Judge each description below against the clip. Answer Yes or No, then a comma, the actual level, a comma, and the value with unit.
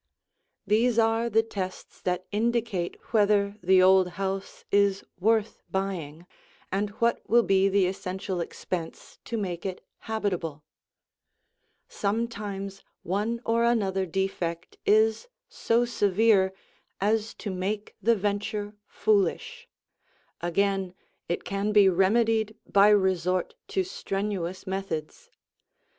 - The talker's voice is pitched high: Yes, high, 200 Hz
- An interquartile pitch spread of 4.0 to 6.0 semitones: No, average, 2.7 semitones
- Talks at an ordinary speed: No, slow, 110 wpm